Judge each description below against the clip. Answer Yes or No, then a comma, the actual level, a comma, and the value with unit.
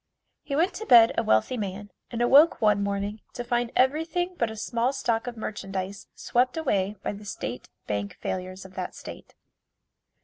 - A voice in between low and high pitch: No, high, 220 Hz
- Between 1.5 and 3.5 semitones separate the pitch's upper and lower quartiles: No, average, 4.5 semitones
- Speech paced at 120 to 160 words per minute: No, average, 175 wpm